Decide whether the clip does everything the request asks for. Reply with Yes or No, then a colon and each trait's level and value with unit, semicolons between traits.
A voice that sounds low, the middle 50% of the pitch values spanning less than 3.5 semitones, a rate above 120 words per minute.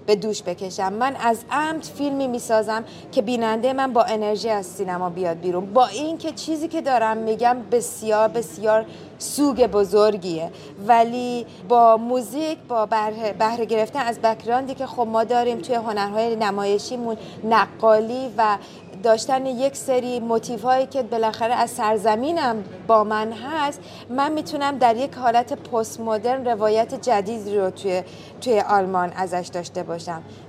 No: high, 225 Hz; average, 3.0 semitones; average, 145 wpm